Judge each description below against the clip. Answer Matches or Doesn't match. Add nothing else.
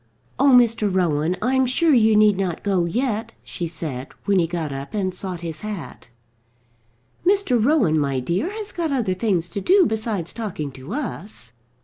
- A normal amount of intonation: Doesn't match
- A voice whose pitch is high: Matches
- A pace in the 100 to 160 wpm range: Doesn't match